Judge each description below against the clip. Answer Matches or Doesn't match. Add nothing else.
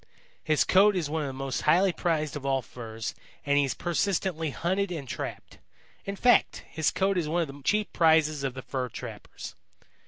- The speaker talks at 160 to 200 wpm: Matches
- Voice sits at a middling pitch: Matches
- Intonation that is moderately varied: Matches